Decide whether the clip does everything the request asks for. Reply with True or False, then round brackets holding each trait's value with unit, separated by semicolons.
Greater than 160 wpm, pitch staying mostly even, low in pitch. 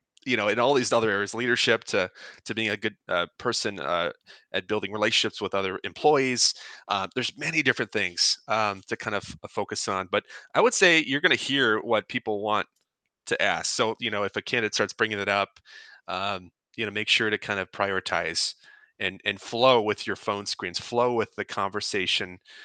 True (200 wpm; 1.9 semitones; 105 Hz)